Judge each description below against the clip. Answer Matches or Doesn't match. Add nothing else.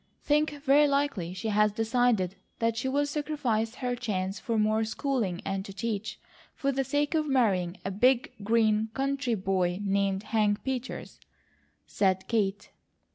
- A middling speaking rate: Matches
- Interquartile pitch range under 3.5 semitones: Doesn't match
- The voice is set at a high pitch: Matches